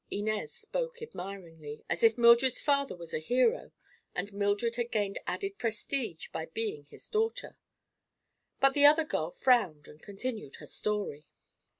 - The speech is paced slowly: No, average, 145 wpm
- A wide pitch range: Yes, wide, 7.4 semitones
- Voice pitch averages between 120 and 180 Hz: No, high, 220 Hz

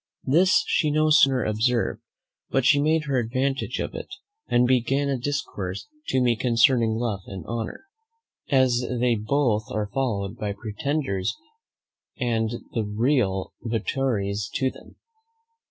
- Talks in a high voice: No, low, 120 Hz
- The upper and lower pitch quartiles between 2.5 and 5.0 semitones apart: Yes, average, 3.9 semitones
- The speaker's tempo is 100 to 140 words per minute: Yes, slow, 135 wpm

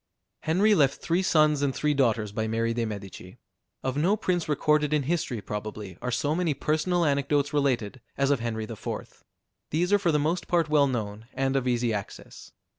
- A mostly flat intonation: No, average, 5.1 semitones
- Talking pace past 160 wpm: Yes, average, 190 wpm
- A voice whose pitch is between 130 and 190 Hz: Yes, medium, 140 Hz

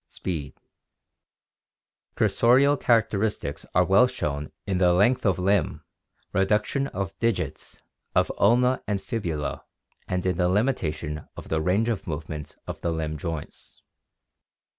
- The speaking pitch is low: Yes, very low, 95 Hz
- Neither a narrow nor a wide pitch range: No, wide, 6.0 semitones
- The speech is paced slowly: Yes, slow, 130 wpm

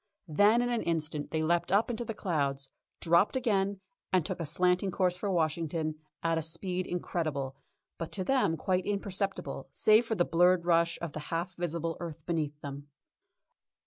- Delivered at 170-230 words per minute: Yes, average, 175 wpm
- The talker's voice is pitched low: No, medium, 170 Hz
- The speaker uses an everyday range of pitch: Yes, average, 3.4 semitones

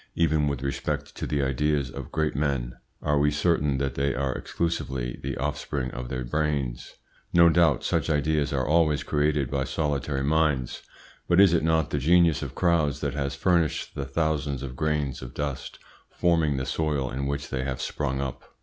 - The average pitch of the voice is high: No, very low, 70 Hz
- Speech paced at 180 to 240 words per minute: Yes, average, 185 wpm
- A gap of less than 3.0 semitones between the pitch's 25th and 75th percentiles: Yes, narrow, 2.5 semitones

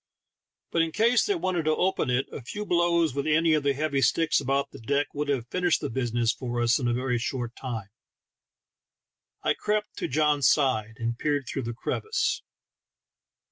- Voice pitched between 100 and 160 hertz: Yes, medium, 140 Hz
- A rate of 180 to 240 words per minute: Yes, average, 185 wpm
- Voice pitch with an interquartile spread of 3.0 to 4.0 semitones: No, average, 5.2 semitones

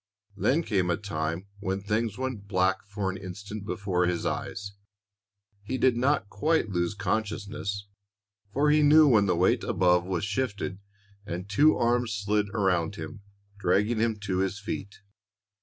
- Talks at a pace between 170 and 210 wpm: No, average, 155 wpm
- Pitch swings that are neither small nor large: Yes, average, 3.0 semitones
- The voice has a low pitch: Yes, low, 100 Hz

